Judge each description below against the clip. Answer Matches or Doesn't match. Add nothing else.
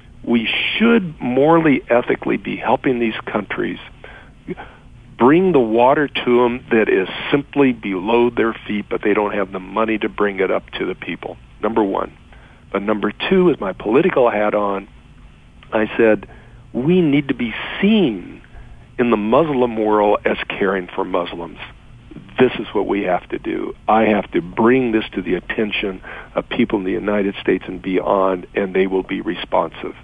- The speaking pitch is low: Matches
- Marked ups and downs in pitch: Doesn't match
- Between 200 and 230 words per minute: Doesn't match